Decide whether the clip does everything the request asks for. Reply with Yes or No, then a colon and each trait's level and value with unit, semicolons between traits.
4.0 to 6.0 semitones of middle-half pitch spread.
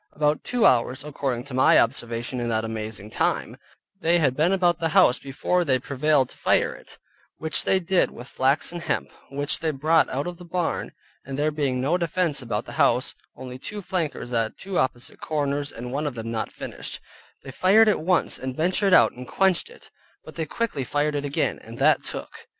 Yes: average, 5.1 semitones